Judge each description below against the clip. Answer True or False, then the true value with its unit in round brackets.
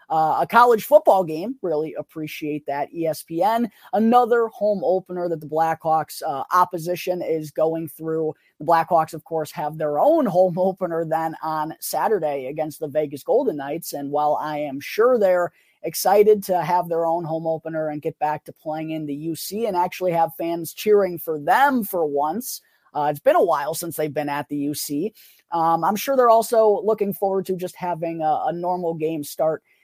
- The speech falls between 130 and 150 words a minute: False (185 wpm)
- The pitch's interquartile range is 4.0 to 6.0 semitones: False (3.4 semitones)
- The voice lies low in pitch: False (165 Hz)